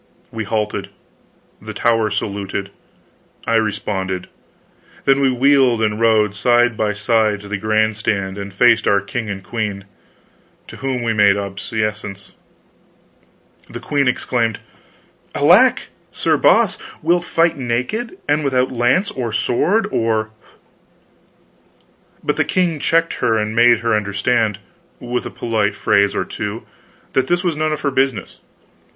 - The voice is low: Yes, low, 115 Hz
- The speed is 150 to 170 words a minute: No, average, 140 wpm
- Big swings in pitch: No, average, 3.7 semitones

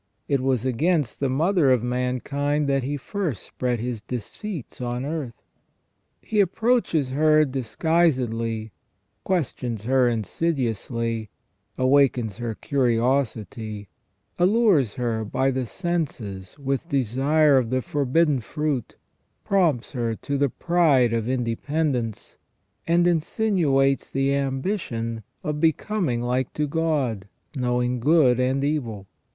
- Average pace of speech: No, slow, 115 wpm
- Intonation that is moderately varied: Yes, average, 4.3 semitones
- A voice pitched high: No, low, 135 Hz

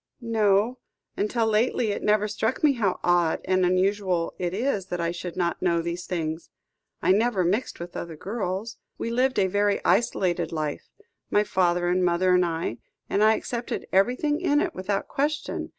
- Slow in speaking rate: No, average, 175 wpm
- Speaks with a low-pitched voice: No, high, 190 Hz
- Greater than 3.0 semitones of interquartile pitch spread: Yes, average, 4.0 semitones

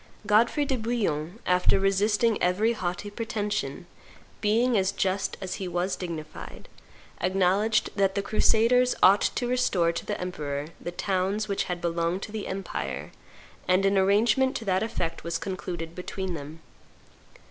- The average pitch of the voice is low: No, high, 195 Hz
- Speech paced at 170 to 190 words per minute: No, average, 145 wpm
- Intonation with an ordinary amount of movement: Yes, average, 3.3 semitones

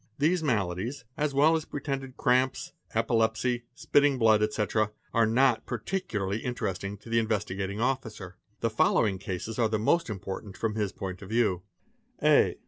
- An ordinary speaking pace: Yes, average, 150 wpm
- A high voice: No, low, 115 Hz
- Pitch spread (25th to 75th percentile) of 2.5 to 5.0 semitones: Yes, average, 4.0 semitones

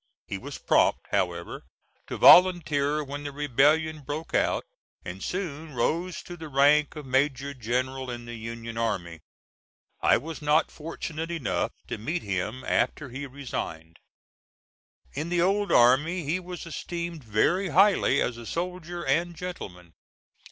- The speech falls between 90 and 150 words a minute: Yes, average, 145 wpm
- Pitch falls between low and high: Yes, medium, 145 Hz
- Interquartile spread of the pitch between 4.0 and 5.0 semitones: No, wide, 5.5 semitones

